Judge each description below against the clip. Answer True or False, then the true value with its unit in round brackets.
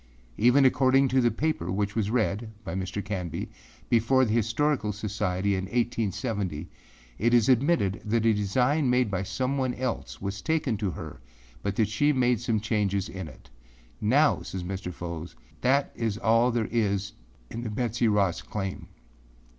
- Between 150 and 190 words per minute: True (160 wpm)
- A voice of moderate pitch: False (110 Hz)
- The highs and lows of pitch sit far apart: False (4.1 semitones)